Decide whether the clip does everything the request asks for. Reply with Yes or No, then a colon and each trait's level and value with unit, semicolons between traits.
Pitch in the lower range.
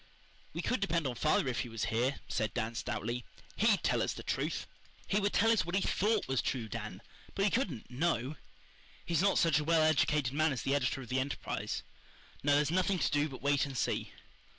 No: medium, 145 Hz